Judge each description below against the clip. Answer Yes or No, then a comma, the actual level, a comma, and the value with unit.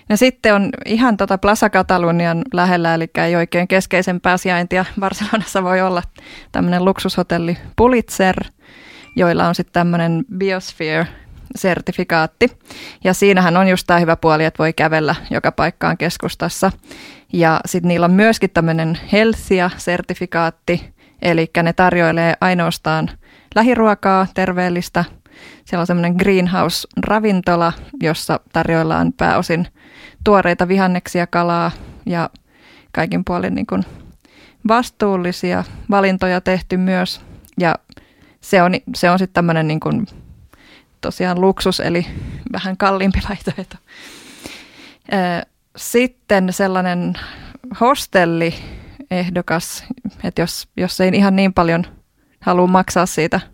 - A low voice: No, medium, 185 Hz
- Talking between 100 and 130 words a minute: Yes, average, 110 wpm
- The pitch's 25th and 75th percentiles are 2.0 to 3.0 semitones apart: Yes, narrow, 2.4 semitones